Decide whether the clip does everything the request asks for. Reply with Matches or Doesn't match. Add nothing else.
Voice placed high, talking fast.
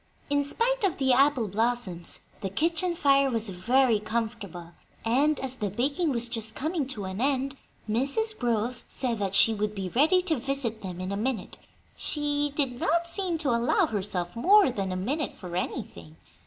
Doesn't match